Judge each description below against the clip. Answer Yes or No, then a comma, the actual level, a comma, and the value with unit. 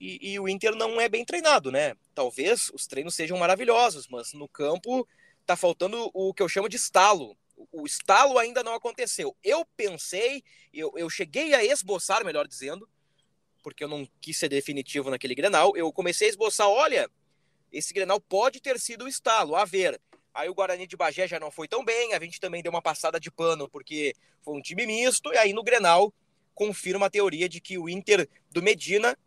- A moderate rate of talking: No, fast, 200 wpm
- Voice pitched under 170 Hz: No, high, 195 Hz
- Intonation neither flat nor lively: No, wide, 6.6 semitones